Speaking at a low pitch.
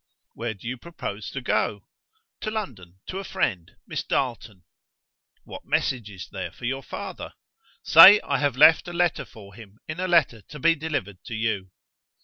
Yes: low, 120 Hz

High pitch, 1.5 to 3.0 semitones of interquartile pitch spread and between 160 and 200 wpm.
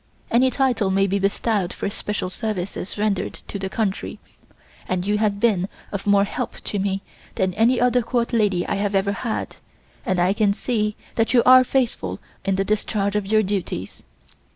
Yes: high, 205 Hz; narrow, 2.5 semitones; average, 180 wpm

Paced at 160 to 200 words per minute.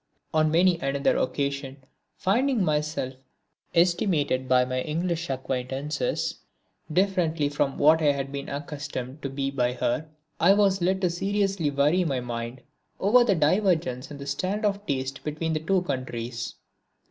No: average, 145 wpm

